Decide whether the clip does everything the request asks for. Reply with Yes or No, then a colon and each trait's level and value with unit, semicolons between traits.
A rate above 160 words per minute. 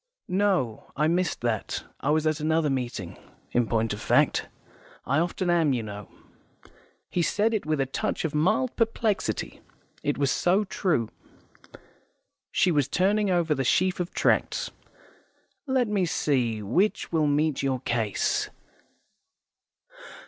No: average, 140 wpm